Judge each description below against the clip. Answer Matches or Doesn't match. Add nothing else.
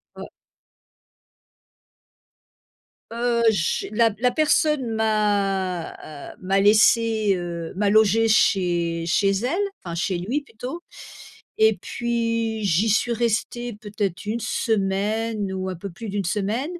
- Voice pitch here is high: Matches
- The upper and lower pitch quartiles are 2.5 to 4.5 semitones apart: Matches